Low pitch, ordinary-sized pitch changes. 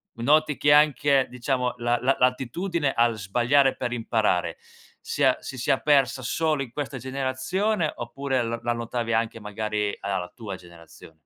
Yes: low, 125 Hz; average, 3.4 semitones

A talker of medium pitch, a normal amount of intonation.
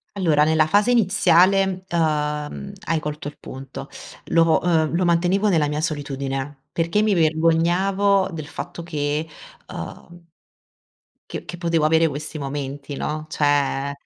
Yes: medium, 160 Hz; average, 3.0 semitones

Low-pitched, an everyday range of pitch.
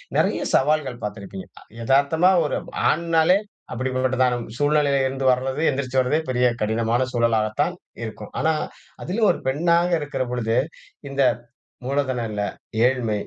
Yes: low, 130 Hz; average, 3.9 semitones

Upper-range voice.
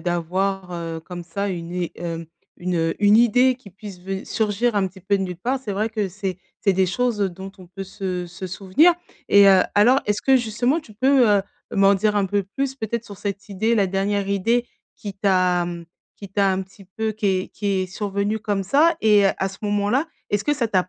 Yes: high, 200 Hz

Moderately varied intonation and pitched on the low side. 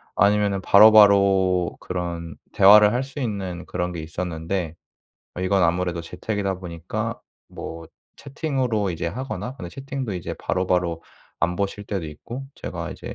Yes: average, 3.2 semitones; very low, 95 Hz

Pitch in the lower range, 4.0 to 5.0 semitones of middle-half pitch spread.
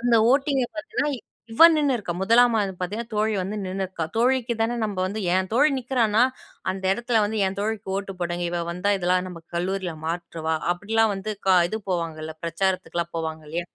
No: high, 195 Hz; average, 4.5 semitones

